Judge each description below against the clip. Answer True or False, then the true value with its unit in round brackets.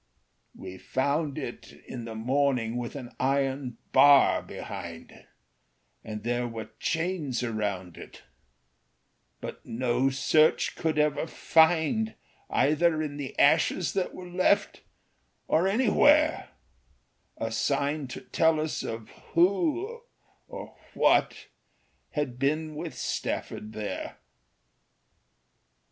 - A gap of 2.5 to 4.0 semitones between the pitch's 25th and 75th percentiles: False (5.1 semitones)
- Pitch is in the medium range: True (145 Hz)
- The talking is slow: True (105 wpm)